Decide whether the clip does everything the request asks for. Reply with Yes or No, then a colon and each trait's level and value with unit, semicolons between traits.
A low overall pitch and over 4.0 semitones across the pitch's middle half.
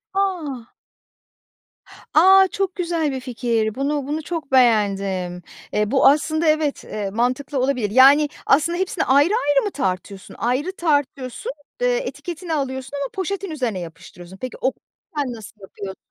No: very high, 275 Hz; wide, 5.5 semitones